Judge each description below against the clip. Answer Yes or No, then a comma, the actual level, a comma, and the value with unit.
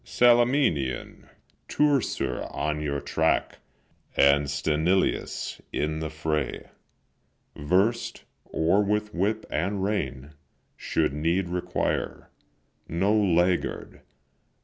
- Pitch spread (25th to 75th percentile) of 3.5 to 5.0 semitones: No, wide, 5.5 semitones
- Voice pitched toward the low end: Yes, very low, 85 Hz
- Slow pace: Yes, slow, 85 wpm